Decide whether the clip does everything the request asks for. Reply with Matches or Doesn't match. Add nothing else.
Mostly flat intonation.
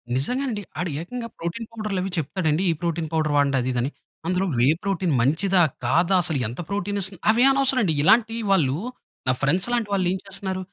Doesn't match